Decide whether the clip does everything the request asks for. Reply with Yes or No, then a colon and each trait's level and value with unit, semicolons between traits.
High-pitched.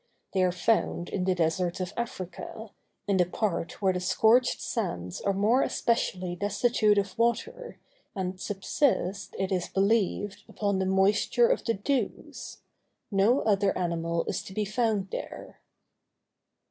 Yes: high, 195 Hz